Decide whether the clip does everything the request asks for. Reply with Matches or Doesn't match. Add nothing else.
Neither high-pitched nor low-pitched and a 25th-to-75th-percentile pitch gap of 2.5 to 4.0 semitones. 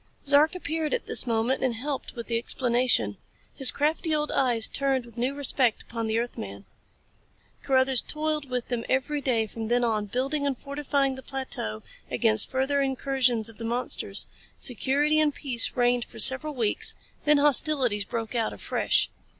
Doesn't match